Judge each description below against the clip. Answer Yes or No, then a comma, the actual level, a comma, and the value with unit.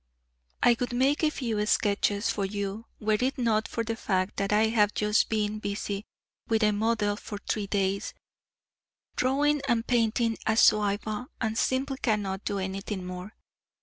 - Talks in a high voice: Yes, high, 215 Hz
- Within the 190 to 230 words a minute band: No, average, 160 wpm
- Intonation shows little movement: Yes, narrow, 2.3 semitones